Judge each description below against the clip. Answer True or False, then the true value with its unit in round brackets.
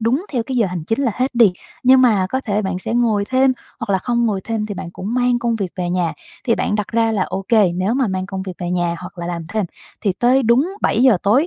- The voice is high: True (220 Hz)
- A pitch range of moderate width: True (4.4 semitones)